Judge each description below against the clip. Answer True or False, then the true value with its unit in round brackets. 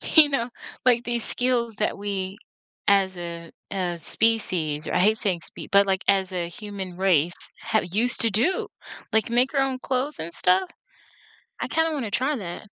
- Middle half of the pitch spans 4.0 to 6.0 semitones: True (4.7 semitones)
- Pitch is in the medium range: False (205 Hz)